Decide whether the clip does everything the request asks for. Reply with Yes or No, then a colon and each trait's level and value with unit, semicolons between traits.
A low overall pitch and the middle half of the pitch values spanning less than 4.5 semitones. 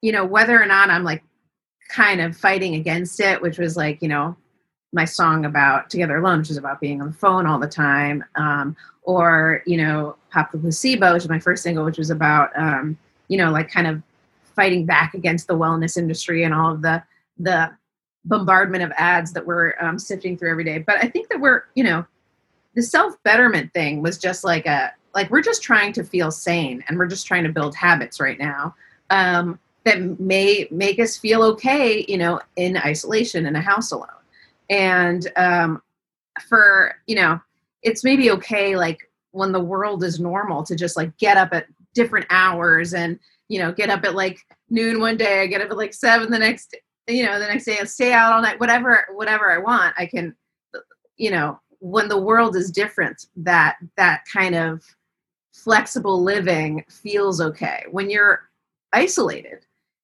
No: medium, 180 Hz; average, 4.1 semitones